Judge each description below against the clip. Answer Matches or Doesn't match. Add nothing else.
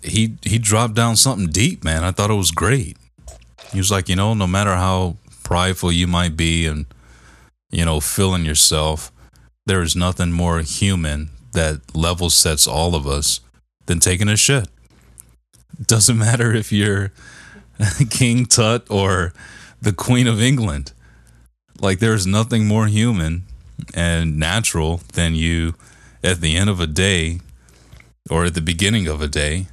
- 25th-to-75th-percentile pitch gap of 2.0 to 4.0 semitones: Doesn't match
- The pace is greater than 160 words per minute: Doesn't match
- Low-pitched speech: Matches